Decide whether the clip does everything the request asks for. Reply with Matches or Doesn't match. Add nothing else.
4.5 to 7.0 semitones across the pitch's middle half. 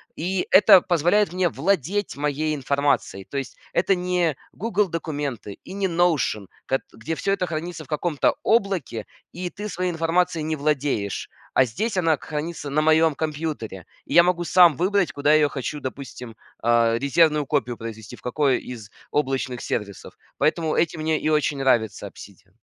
Matches